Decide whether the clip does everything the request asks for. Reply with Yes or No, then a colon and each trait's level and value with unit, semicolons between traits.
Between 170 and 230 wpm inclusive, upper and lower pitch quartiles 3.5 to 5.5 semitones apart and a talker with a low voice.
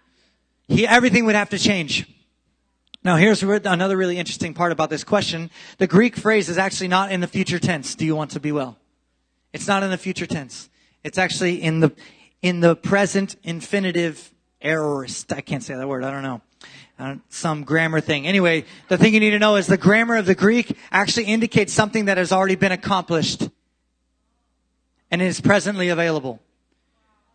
No: average, 185 wpm; average, 4.1 semitones; medium, 180 Hz